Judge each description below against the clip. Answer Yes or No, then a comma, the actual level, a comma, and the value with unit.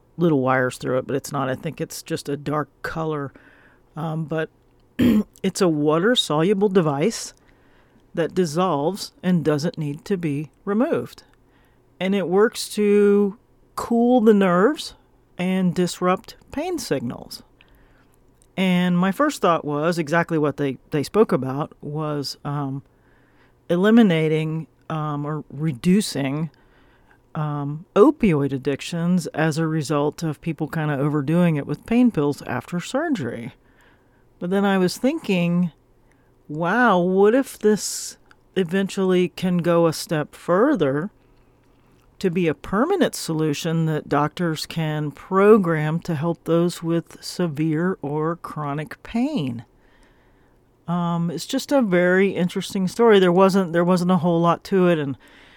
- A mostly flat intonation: No, average, 4.6 semitones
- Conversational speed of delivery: No, slow, 130 wpm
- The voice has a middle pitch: Yes, medium, 165 Hz